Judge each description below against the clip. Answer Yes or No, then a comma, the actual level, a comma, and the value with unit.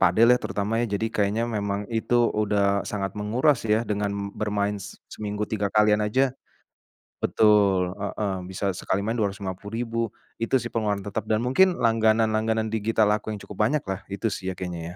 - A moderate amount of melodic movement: No, narrow, 2.0 semitones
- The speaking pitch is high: No, low, 105 Hz